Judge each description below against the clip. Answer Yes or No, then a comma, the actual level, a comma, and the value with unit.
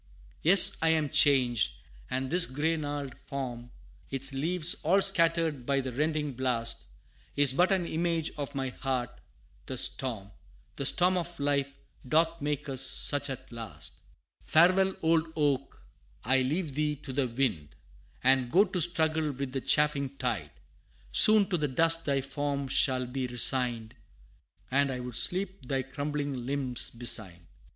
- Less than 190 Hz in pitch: Yes, medium, 140 Hz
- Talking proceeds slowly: No, average, 150 wpm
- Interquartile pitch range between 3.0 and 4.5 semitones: Yes, average, 3.8 semitones